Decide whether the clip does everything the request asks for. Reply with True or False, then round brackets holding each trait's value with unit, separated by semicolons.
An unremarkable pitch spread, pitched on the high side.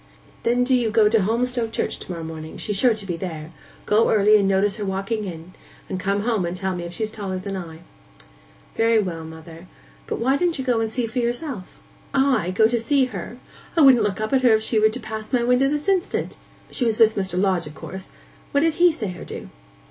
True (4.6 semitones; 215 Hz)